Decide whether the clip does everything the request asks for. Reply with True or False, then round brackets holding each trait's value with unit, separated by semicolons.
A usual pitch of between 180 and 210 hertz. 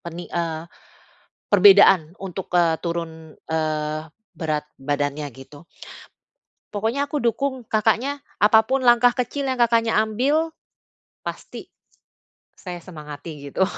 True (185 Hz)